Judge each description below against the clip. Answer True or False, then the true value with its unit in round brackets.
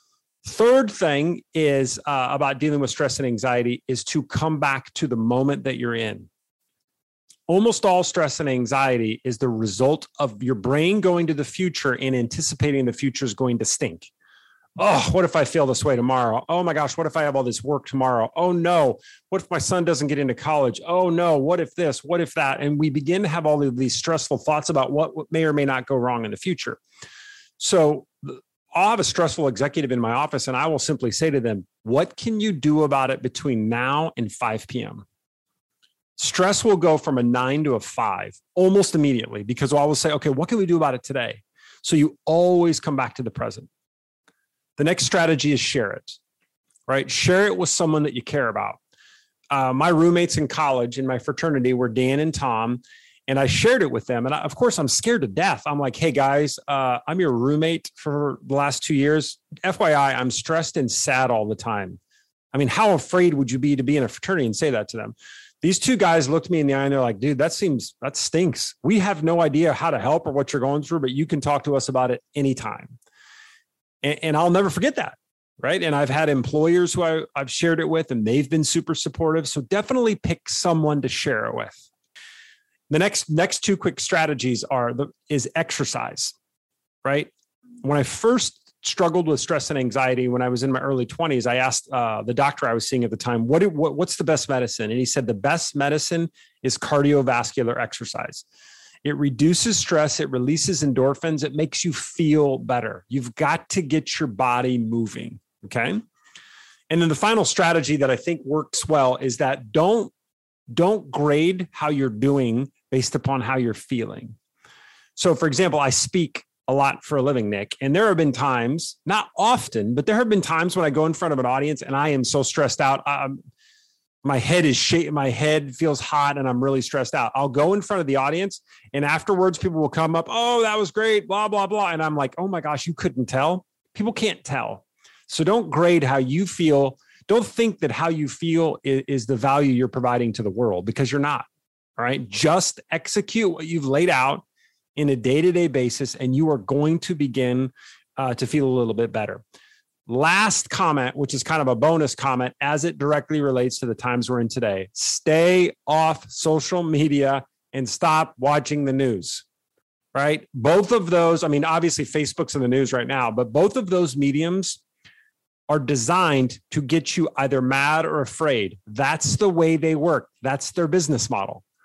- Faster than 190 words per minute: True (205 wpm)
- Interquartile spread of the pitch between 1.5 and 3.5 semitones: False (4.3 semitones)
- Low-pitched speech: False (145 Hz)